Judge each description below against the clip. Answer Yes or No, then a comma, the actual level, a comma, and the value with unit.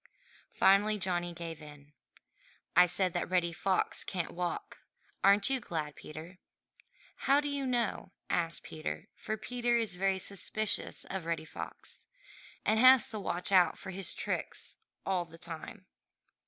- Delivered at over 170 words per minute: No, average, 145 wpm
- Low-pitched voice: No, medium, 185 Hz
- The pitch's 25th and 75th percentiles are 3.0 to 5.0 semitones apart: Yes, average, 4.2 semitones